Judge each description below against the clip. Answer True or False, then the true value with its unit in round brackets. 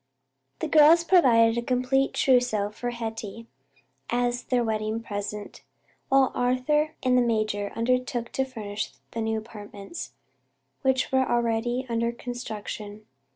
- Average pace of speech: False (125 wpm)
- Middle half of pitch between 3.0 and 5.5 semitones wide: False (2.6 semitones)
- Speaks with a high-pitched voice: True (235 Hz)